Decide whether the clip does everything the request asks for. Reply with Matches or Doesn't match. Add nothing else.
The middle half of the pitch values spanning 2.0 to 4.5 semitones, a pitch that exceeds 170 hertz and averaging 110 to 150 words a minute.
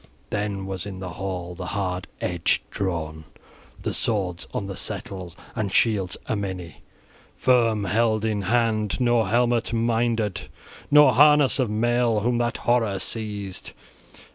Doesn't match